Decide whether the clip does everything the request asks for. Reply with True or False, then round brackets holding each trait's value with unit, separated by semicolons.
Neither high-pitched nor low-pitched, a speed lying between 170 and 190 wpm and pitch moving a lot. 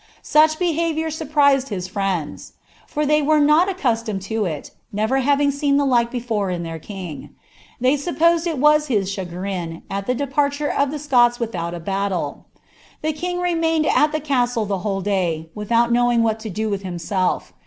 False (240 Hz; 175 wpm; 7.3 semitones)